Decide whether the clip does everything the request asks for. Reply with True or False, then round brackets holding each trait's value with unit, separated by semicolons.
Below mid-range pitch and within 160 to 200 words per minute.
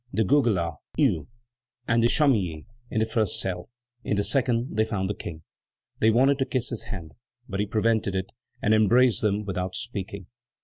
True (105 Hz; 180 wpm)